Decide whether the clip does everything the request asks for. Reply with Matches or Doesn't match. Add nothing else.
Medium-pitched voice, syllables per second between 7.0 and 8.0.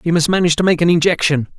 Matches